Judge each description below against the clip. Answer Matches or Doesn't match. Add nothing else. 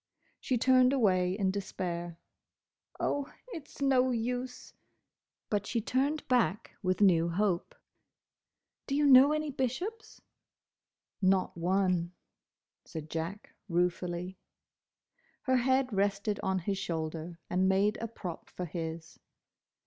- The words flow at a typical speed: Doesn't match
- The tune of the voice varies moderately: Doesn't match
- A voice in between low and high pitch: Doesn't match